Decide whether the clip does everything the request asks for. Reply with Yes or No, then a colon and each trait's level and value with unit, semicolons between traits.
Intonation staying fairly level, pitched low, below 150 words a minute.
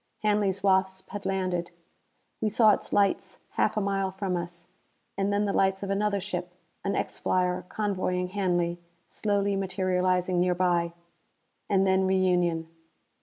No: narrow, 1.7 semitones; high, 190 Hz; average, 140 wpm